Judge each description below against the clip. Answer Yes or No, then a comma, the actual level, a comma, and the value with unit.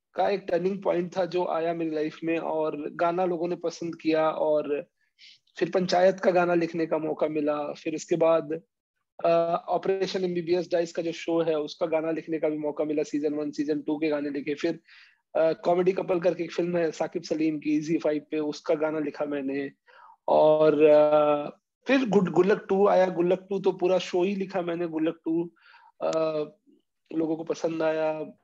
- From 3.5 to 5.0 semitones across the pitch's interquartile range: No, narrow, 2.6 semitones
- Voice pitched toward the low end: No, medium, 165 Hz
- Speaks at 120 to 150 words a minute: No, average, 185 wpm